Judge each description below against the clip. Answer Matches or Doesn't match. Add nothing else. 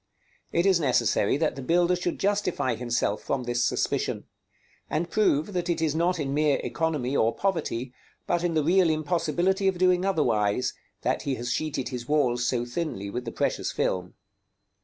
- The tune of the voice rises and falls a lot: Matches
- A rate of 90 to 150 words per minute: Doesn't match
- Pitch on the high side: Doesn't match